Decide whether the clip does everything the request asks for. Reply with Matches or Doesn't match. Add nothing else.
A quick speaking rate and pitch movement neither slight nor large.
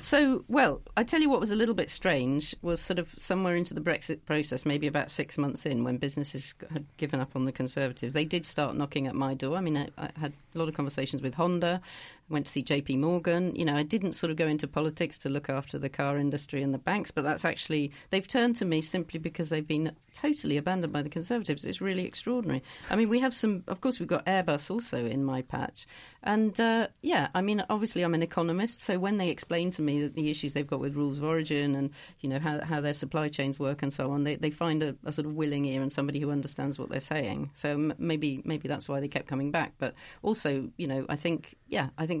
Matches